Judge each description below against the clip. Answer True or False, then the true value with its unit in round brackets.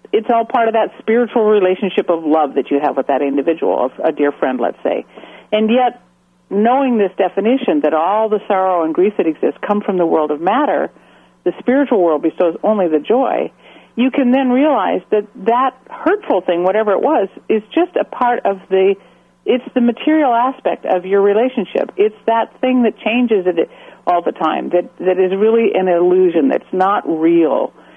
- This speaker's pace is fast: False (190 wpm)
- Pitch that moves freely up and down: True (5.8 semitones)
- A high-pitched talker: True (210 Hz)